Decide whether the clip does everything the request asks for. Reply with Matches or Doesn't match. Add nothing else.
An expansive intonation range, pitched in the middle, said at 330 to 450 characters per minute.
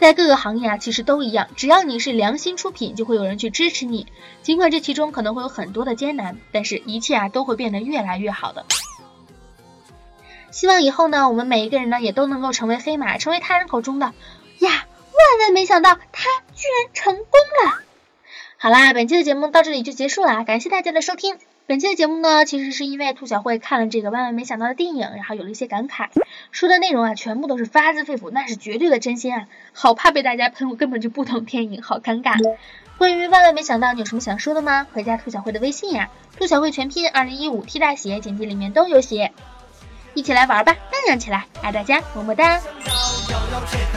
Doesn't match